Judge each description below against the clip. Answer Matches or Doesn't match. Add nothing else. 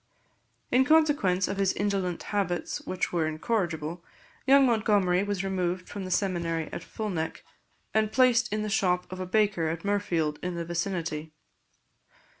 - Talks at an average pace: Matches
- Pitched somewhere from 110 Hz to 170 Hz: Doesn't match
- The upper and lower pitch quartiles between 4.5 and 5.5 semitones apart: Doesn't match